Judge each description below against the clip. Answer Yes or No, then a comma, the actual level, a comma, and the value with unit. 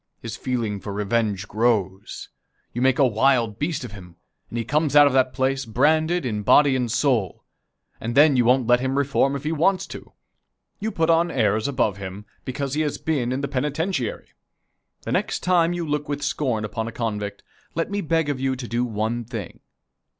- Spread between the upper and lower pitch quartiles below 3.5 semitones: No, average, 4.6 semitones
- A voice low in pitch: Yes, low, 130 Hz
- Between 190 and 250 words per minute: Yes, average, 200 wpm